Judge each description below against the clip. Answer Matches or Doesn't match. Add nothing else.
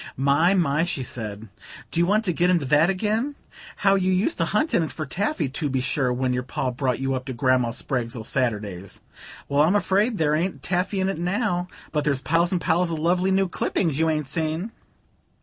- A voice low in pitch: Doesn't match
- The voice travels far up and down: Matches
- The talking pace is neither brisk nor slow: Doesn't match